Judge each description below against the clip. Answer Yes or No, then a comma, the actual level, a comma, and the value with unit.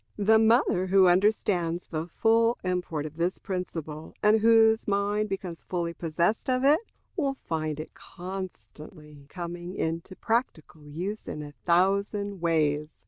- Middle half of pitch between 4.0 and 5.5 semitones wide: Yes, average, 4.3 semitones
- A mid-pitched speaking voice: Yes, medium, 180 Hz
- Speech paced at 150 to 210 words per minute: No, average, 140 wpm